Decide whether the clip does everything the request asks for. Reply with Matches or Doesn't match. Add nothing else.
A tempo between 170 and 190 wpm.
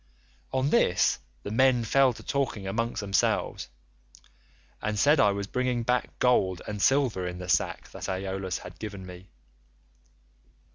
Doesn't match